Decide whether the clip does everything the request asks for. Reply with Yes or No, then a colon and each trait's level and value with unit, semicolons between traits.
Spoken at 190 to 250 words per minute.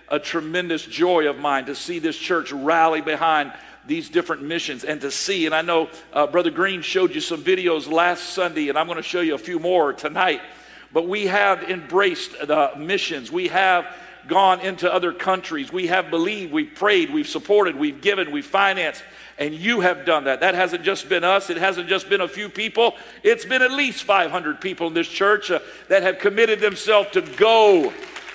Yes: average, 200 wpm